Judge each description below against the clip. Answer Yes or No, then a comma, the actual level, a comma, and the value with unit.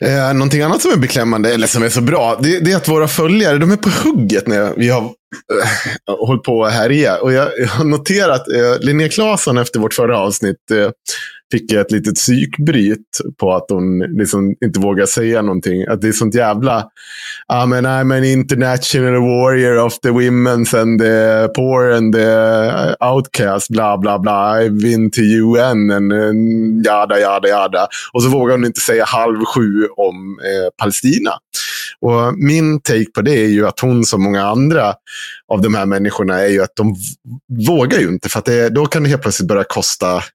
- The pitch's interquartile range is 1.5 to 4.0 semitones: Yes, average, 3.4 semitones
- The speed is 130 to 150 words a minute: No, average, 190 wpm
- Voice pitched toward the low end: Yes, low, 115 Hz